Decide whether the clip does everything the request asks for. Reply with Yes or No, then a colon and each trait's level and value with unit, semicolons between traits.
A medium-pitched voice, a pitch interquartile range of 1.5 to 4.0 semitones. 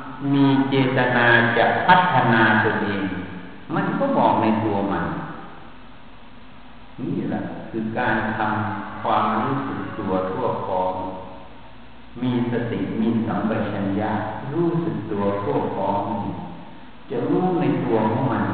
No: low, 110 Hz; average, 3.7 semitones